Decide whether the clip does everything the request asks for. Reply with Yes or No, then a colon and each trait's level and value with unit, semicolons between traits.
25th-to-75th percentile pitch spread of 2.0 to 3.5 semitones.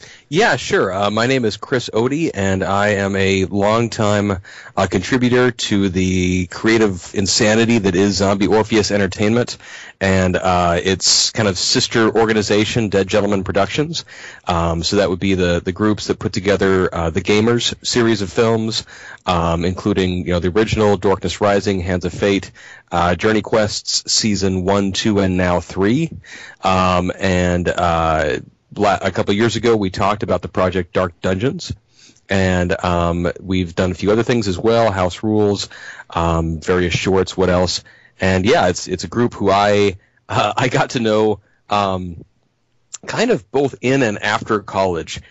Yes: average, 2.8 semitones